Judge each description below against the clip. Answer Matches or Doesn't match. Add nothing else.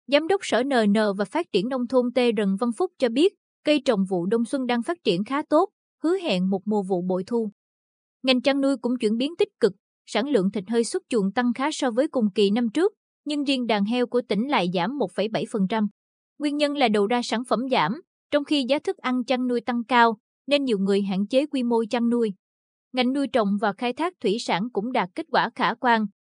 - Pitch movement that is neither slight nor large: Matches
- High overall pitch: Matches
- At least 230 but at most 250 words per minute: Matches